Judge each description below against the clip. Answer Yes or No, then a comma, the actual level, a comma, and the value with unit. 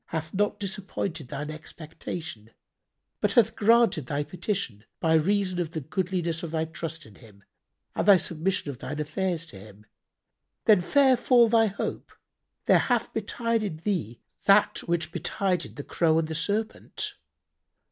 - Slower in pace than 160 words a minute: Yes, average, 150 wpm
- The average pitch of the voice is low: No, medium, 170 Hz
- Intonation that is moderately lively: Yes, average, 4.6 semitones